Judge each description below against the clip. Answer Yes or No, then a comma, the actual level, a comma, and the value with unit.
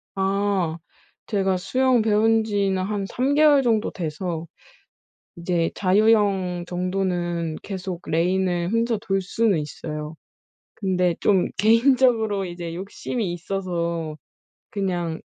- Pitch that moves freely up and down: No, average, 3.6 semitones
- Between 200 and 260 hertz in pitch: No, high, 190 Hz